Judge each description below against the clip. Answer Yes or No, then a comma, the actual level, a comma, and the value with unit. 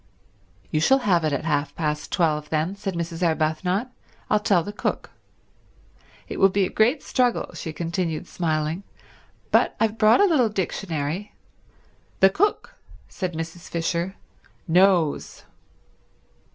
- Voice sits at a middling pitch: Yes, medium, 175 Hz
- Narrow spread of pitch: No, average, 4.2 semitones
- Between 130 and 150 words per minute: Yes, slow, 135 wpm